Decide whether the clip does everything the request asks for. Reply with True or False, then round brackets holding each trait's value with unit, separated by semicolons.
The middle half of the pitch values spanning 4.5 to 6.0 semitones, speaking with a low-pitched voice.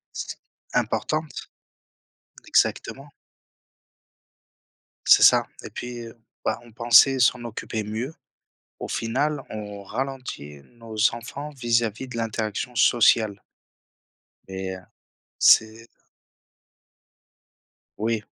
False (2.8 semitones; 115 Hz)